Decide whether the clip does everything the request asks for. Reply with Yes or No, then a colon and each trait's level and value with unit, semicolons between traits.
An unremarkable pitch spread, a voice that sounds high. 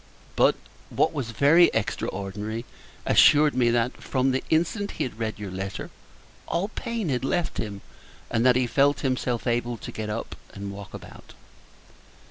No: average, 4.7 semitones; low, 120 Hz